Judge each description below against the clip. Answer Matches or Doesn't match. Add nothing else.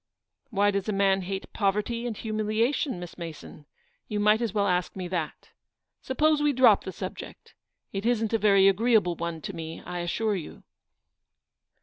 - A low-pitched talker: Doesn't match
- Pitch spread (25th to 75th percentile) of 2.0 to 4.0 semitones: Matches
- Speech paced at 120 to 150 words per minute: Doesn't match